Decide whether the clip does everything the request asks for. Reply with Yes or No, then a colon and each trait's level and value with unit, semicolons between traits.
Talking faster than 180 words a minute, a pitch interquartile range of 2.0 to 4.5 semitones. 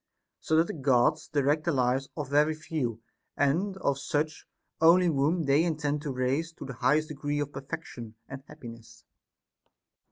No: average, 165 wpm; narrow, 2.6 semitones